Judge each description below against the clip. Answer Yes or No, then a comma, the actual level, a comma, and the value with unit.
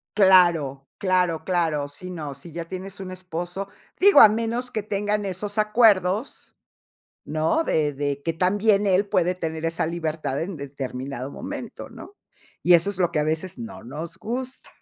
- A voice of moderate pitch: Yes, medium, 180 Hz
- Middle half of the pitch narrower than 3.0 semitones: No, average, 4.4 semitones